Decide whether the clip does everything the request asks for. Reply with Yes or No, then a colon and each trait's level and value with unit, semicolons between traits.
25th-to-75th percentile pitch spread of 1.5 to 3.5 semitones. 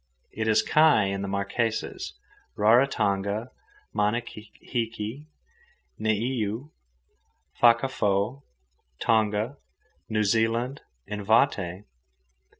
Yes: narrow, 2.6 semitones